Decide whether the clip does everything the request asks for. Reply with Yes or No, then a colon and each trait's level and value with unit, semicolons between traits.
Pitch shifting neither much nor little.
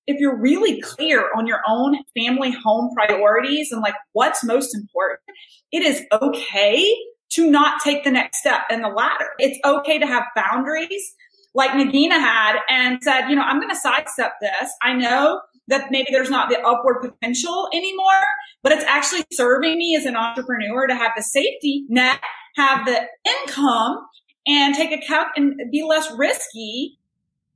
Yes: average, 4.2 semitones